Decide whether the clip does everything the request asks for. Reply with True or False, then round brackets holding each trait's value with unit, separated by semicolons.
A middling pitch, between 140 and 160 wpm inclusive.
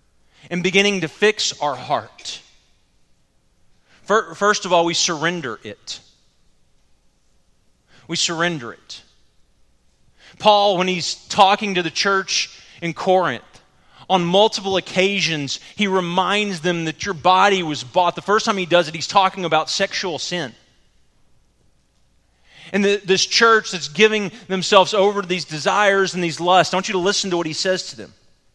True (180 Hz; 150 wpm)